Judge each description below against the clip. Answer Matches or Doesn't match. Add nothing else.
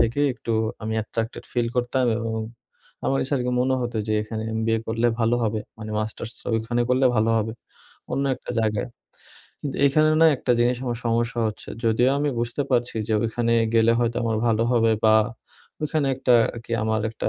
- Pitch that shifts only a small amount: Matches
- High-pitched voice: Doesn't match